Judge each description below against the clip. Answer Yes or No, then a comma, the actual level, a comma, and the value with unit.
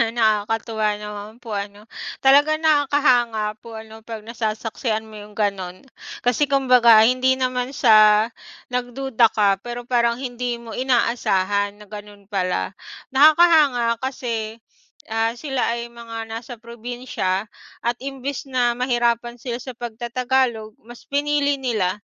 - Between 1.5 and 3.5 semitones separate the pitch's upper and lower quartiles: Yes, average, 2.8 semitones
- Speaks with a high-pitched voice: Yes, high, 235 Hz